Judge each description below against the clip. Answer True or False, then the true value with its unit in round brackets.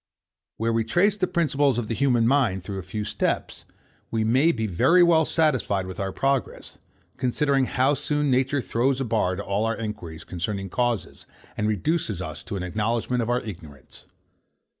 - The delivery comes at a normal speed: True (180 wpm)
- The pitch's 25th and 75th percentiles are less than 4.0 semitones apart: False (5.4 semitones)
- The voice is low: True (115 Hz)